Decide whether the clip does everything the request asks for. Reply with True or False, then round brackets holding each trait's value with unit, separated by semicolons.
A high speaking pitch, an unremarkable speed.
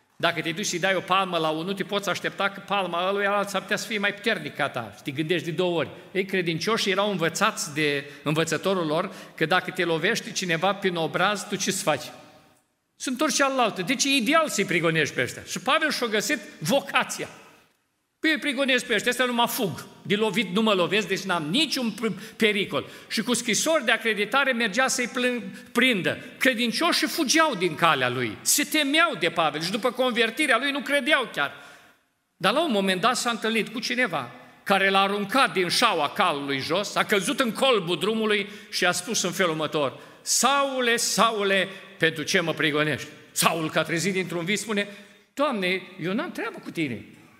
False (200 Hz; 190 wpm)